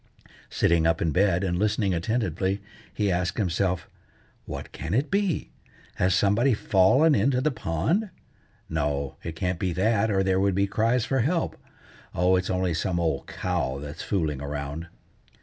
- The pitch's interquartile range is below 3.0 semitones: No, average, 4.8 semitones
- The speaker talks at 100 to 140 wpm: No, average, 160 wpm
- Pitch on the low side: Yes, very low, 95 Hz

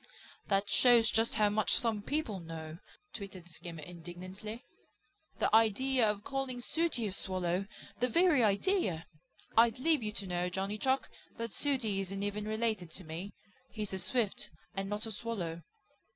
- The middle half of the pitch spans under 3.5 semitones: No, average, 3.9 semitones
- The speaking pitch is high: Yes, high, 210 Hz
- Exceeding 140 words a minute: Yes, average, 155 wpm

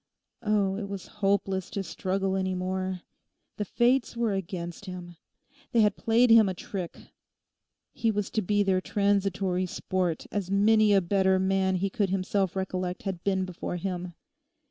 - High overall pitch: Yes, high, 195 Hz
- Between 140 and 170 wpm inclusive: Yes, average, 160 wpm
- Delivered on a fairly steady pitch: Yes, narrow, 1.7 semitones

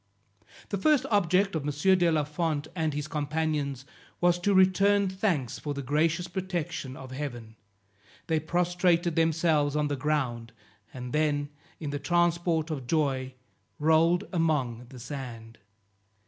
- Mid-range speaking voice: Yes, medium, 155 Hz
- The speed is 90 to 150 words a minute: Yes, average, 140 wpm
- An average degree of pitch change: Yes, average, 3.6 semitones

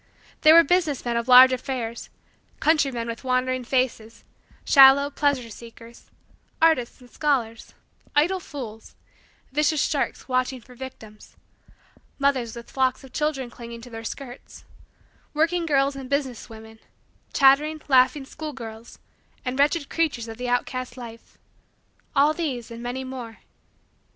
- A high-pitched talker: Yes, very high, 255 Hz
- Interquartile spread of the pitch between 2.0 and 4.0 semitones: Yes, average, 3.3 semitones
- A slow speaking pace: Yes, slow, 130 wpm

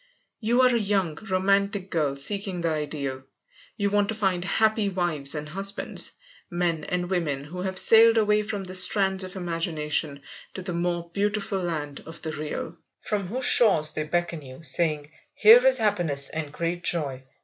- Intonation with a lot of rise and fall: No, average, 4.6 semitones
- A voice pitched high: No, medium, 180 Hz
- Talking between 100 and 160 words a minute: No, average, 170 wpm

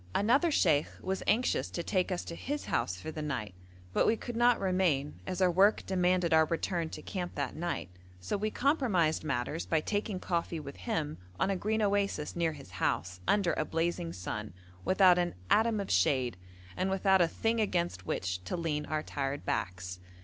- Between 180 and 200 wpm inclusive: Yes, average, 190 wpm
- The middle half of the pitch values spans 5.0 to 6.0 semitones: Yes, wide, 5.4 semitones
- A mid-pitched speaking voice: Yes, medium, 170 Hz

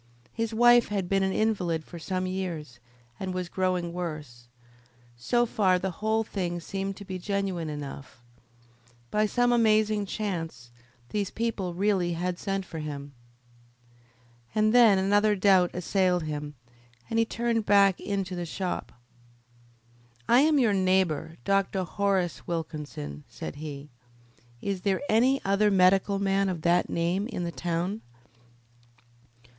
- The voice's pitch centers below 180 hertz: No, high, 190 Hz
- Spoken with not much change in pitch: No, average, 3.3 semitones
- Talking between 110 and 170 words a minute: Yes, average, 140 wpm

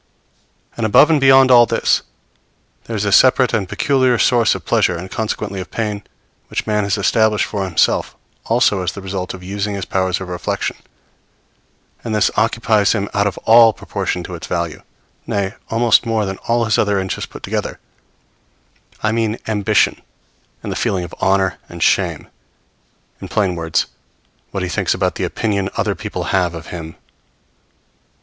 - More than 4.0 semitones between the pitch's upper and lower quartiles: No, average, 3.1 semitones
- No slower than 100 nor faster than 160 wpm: No, average, 170 wpm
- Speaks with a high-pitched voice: No, low, 100 Hz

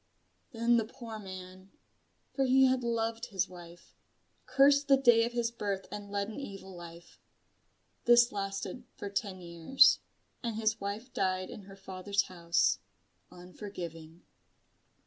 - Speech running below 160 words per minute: Yes, average, 140 wpm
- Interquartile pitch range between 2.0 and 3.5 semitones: No, average, 4.2 semitones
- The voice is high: Yes, high, 205 Hz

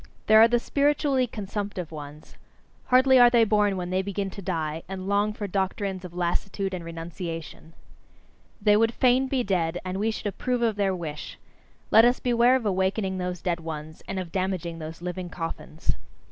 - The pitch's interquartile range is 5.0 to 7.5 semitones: No, average, 4.2 semitones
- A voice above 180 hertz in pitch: Yes, high, 190 Hz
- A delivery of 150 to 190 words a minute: Yes, average, 180 wpm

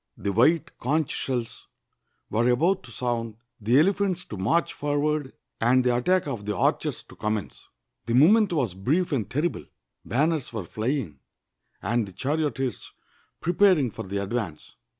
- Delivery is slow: No, average, 150 wpm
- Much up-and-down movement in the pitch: Yes, wide, 5.8 semitones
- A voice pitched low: Yes, low, 130 Hz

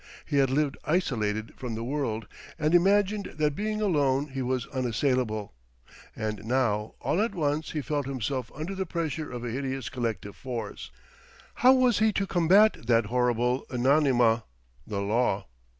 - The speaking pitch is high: No, low, 130 Hz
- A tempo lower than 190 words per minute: Yes, average, 155 wpm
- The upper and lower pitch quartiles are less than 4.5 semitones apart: No, average, 5.3 semitones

